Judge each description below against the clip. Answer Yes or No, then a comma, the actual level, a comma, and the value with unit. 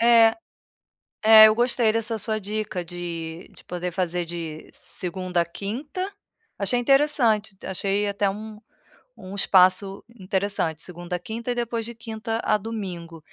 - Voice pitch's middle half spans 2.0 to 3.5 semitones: No, average, 4.0 semitones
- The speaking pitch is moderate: No, high, 205 Hz